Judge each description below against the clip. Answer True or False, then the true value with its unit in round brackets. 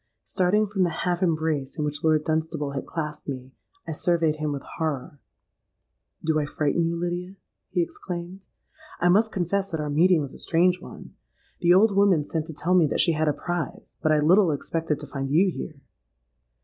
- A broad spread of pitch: False (3.0 semitones)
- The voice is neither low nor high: True (165 Hz)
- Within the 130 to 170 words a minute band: False (195 wpm)